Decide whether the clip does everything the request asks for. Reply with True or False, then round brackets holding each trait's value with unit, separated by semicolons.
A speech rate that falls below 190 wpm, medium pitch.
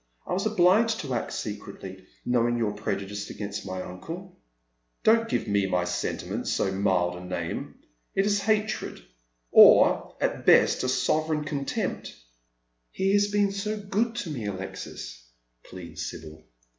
False (160 wpm; 115 Hz)